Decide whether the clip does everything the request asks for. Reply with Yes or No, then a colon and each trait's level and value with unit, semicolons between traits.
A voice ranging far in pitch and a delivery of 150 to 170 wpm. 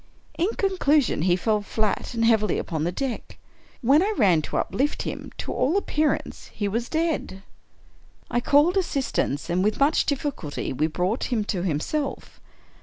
Yes: wide, 7.8 semitones; average, 160 wpm